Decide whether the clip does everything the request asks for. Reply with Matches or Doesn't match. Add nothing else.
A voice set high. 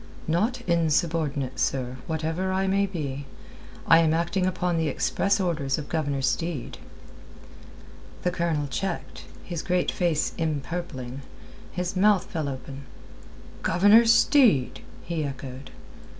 Doesn't match